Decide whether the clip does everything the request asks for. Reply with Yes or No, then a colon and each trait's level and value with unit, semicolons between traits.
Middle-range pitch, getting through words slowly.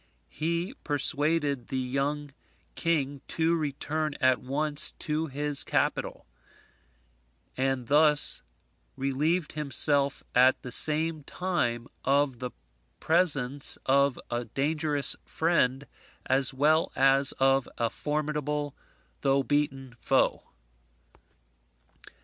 Yes: medium, 145 Hz; slow, 95 wpm